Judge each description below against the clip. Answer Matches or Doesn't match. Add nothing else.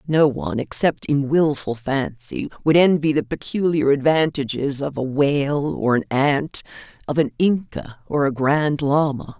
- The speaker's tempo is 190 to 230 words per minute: Doesn't match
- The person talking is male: Doesn't match